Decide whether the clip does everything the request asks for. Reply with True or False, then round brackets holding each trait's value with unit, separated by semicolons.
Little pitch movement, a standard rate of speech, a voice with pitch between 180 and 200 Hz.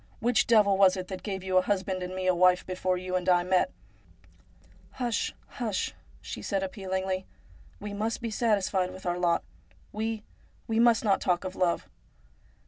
True (2.3 semitones; 195 wpm; 190 Hz)